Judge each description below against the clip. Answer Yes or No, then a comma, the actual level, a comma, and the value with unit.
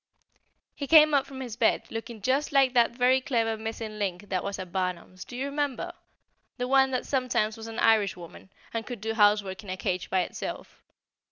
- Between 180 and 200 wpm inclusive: Yes, average, 195 wpm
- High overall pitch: Yes, high, 225 Hz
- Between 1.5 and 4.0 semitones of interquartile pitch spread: No, average, 4.5 semitones